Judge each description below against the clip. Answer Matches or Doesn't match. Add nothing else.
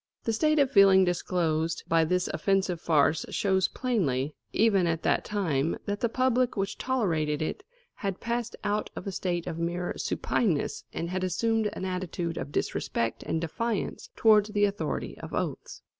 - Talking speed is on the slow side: Doesn't match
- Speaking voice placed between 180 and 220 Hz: Matches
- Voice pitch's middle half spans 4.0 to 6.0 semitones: Matches